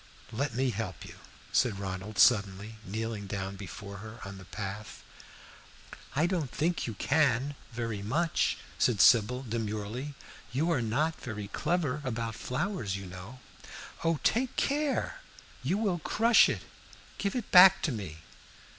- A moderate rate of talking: Yes, average, 145 wpm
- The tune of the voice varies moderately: No, wide, 7.1 semitones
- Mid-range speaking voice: No, low, 115 Hz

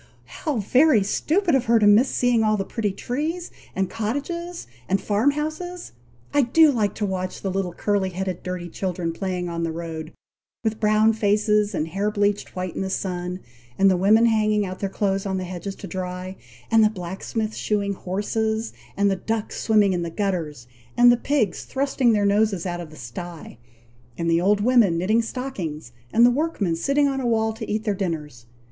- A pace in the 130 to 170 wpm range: No, average, 195 wpm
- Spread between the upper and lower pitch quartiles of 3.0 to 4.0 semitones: Yes, average, 3.7 semitones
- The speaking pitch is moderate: No, high, 205 Hz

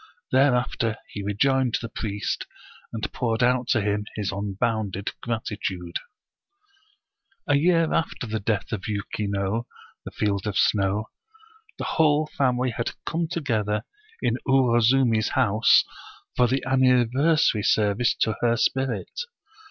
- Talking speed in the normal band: No, slow, 130 wpm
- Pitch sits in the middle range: No, low, 115 Hz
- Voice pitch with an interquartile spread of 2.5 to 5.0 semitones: Yes, average, 3.9 semitones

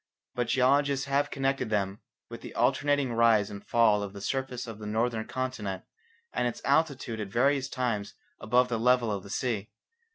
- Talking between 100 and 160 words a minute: No, average, 175 wpm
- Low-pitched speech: Yes, low, 120 Hz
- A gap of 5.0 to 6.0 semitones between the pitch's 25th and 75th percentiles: No, average, 4.0 semitones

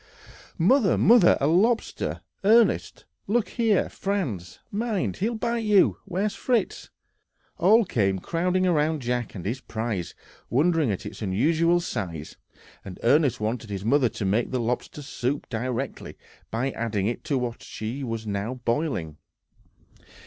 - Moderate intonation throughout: No, wide, 8.6 semitones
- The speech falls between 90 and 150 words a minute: Yes, slow, 135 wpm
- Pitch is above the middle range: No, low, 135 Hz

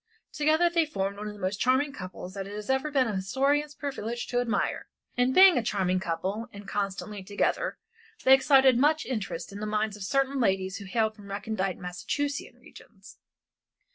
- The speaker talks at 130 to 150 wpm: No, average, 185 wpm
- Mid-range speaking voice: No, high, 220 Hz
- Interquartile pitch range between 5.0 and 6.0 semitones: Yes, wide, 5.6 semitones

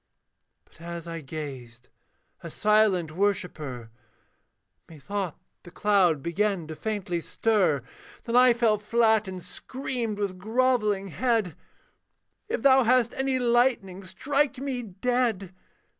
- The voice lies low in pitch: No, high, 205 Hz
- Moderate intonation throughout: No, wide, 5.8 semitones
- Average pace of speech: No, slow, 115 wpm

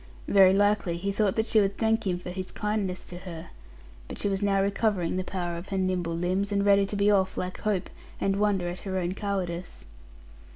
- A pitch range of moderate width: No, narrow, 2.0 semitones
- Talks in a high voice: Yes, high, 195 Hz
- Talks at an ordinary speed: No, fast, 215 wpm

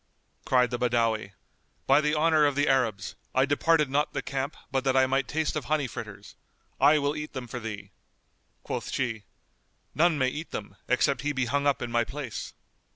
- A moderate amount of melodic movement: Yes, average, 3.3 semitones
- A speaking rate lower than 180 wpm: No, average, 195 wpm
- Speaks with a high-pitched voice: No, low, 135 Hz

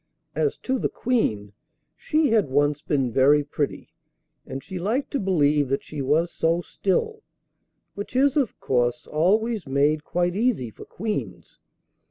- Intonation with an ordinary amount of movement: No, wide, 7.8 semitones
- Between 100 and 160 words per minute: Yes, average, 150 wpm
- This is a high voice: No, medium, 165 Hz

